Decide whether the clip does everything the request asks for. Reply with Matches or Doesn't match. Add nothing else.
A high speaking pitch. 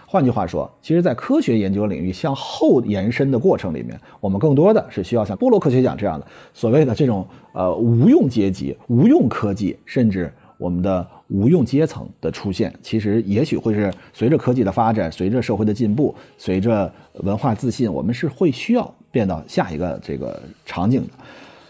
Doesn't match